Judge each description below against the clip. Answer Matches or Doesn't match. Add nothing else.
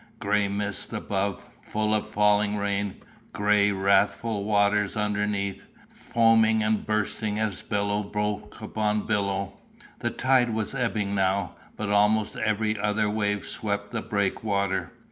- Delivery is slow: Matches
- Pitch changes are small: Matches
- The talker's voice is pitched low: Matches